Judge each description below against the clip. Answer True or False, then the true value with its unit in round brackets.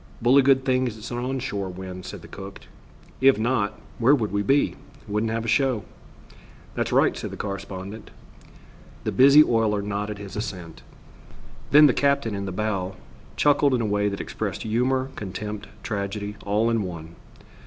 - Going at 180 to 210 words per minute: False (170 wpm)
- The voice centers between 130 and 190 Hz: False (110 Hz)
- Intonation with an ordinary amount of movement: True (4.2 semitones)